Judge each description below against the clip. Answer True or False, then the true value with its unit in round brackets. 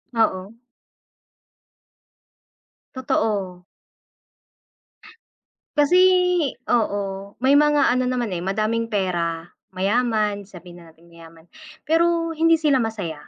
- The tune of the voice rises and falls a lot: True (5.7 semitones)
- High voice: True (210 Hz)